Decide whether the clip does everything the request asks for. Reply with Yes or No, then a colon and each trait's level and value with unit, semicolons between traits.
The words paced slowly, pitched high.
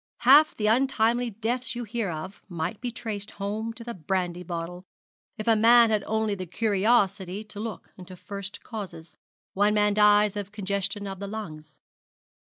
No: average, 165 wpm; high, 210 Hz